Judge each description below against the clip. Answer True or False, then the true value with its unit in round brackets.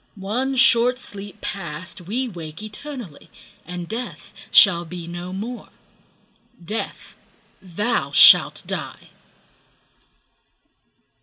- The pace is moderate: False (90 wpm)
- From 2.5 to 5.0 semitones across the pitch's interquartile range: False (5.4 semitones)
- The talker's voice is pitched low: False (200 Hz)